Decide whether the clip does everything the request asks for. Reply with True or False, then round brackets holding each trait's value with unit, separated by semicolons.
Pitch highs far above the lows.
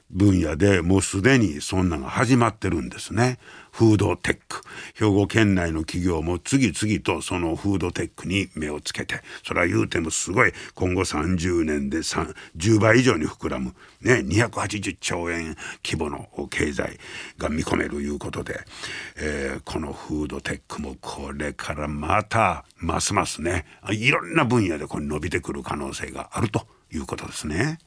True (5.8 semitones)